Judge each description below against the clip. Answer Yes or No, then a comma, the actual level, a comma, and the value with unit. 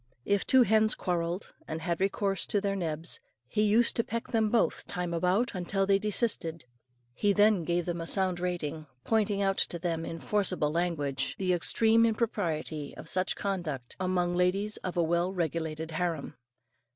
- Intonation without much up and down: No, average, 3.4 semitones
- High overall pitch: No, medium, 180 Hz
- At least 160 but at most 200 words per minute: Yes, average, 170 wpm